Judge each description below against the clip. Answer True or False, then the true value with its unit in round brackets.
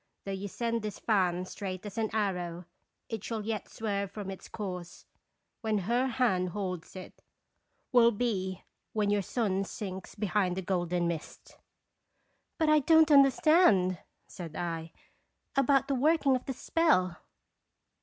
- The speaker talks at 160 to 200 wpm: False (145 wpm)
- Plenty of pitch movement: False (4.6 semitones)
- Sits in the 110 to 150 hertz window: False (205 Hz)